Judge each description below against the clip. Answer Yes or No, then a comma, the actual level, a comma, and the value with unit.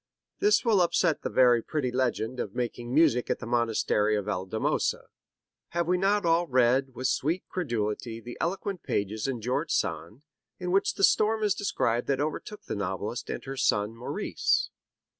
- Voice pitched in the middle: No, low, 130 Hz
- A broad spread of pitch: Yes, wide, 7.2 semitones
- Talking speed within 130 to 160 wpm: No, average, 170 wpm